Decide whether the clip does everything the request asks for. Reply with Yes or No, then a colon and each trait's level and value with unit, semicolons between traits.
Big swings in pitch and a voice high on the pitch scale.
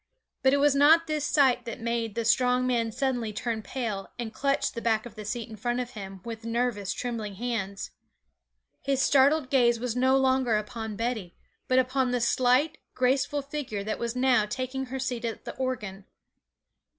No: average, 2.9 semitones; high, 245 Hz